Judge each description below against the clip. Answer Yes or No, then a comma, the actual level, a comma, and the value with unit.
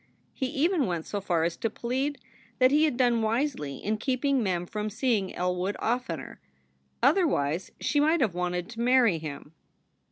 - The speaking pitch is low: No, high, 225 Hz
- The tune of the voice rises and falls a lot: Yes, wide, 6.7 semitones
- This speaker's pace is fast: No, average, 165 wpm